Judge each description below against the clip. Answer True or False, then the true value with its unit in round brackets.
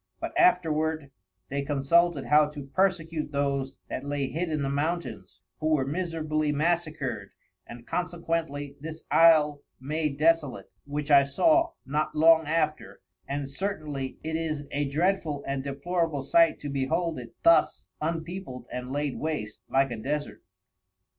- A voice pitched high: False (150 Hz)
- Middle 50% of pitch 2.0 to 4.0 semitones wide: True (2.9 semitones)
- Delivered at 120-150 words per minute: True (140 wpm)